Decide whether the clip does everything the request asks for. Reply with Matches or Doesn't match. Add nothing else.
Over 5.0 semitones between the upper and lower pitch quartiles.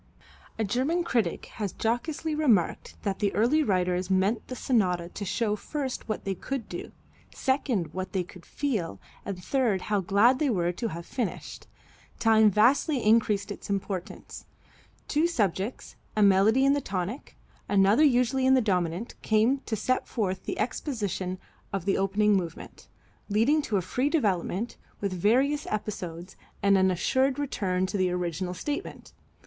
Matches